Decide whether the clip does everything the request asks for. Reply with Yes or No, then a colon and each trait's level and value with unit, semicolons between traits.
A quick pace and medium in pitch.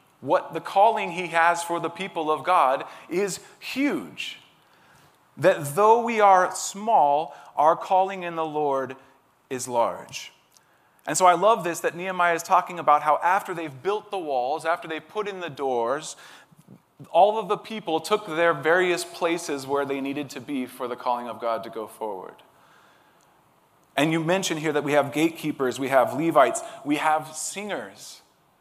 No: average, 170 wpm; medium, 165 Hz